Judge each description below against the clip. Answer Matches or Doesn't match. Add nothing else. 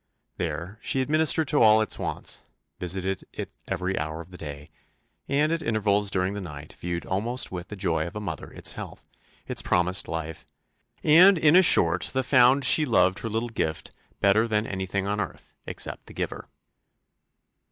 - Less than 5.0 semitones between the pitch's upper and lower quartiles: Doesn't match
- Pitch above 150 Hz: Doesn't match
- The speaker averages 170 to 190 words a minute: Matches